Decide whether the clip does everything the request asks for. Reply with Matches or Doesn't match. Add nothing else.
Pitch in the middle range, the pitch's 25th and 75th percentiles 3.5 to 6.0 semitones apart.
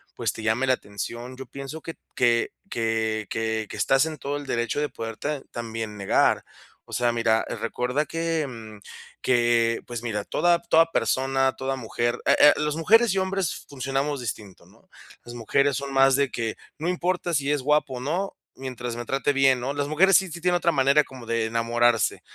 Doesn't match